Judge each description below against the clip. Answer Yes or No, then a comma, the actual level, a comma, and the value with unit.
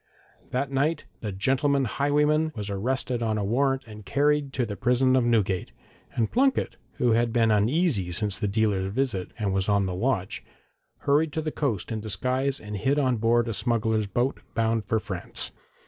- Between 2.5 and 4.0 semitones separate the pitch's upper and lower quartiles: No, average, 4.6 semitones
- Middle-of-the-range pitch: No, low, 115 Hz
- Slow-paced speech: No, average, 180 wpm